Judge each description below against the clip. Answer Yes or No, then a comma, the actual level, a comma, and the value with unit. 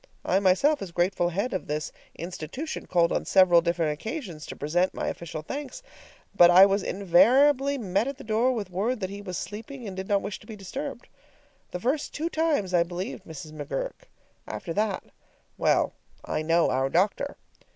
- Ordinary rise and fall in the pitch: No, wide, 6.3 semitones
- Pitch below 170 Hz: No, high, 195 Hz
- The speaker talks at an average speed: Yes, average, 180 wpm